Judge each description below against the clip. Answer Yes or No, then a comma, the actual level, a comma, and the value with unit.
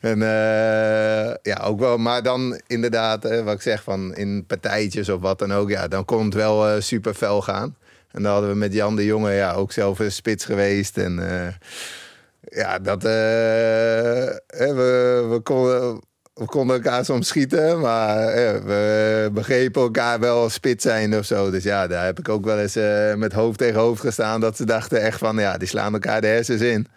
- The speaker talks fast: Yes, fast, 205 wpm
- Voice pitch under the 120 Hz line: Yes, low, 110 Hz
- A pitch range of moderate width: No, narrow, 2.3 semitones